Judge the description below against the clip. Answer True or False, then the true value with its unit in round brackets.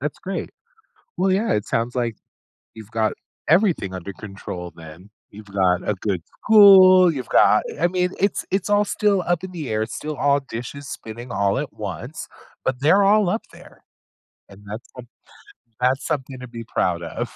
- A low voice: True (125 Hz)